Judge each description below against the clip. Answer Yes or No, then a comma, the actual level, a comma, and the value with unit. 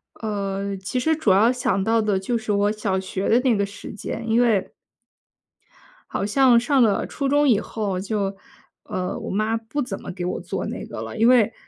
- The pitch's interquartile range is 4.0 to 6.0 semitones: No, average, 3.3 semitones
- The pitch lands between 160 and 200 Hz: No, high, 215 Hz